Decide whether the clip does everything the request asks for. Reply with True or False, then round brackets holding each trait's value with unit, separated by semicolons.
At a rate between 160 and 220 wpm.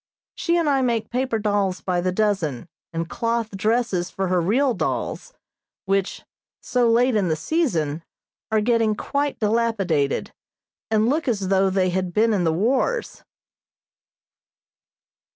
False (140 wpm)